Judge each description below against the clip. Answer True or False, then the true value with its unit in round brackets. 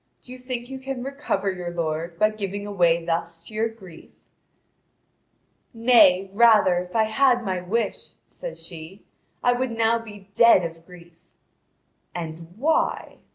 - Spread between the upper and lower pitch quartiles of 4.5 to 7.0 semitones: True (5.3 semitones)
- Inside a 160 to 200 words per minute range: False (150 wpm)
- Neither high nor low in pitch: False (205 Hz)